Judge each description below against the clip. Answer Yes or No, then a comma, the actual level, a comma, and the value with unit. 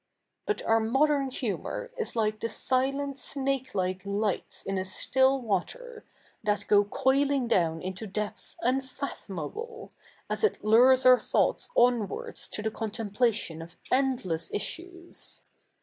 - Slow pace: Yes, slow, 125 wpm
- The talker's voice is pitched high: Yes, high, 240 Hz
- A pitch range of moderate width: Yes, average, 5.0 semitones